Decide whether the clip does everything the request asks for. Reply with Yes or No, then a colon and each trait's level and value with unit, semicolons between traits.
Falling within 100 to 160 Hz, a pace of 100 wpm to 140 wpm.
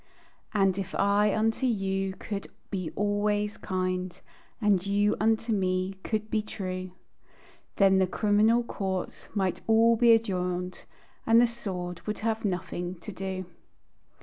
No: high, 200 Hz; slow, 135 wpm